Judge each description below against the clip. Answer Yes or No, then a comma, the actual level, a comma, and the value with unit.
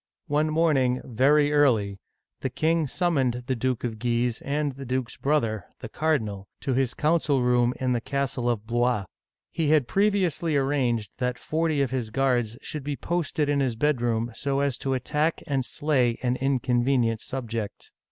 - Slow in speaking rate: No, average, 170 wpm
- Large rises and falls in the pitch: No, average, 3.5 semitones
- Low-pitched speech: Yes, low, 130 Hz